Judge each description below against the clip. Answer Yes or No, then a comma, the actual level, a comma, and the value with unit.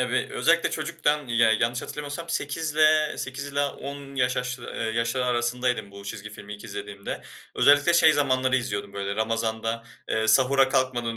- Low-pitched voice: Yes, low, 125 Hz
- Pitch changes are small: No, average, 4.1 semitones